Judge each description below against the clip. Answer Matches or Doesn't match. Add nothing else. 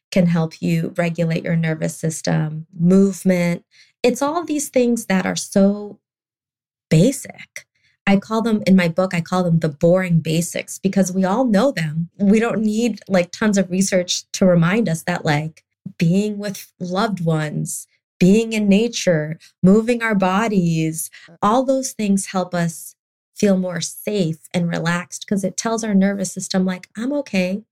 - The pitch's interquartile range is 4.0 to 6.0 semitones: Doesn't match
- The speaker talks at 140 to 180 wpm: Matches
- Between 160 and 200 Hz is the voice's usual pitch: Matches